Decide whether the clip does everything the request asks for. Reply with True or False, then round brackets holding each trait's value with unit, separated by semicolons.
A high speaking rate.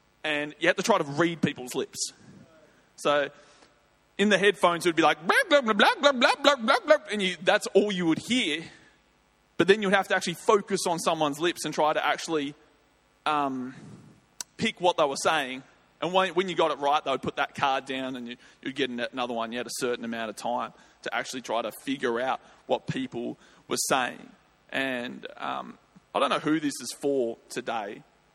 True (210 wpm)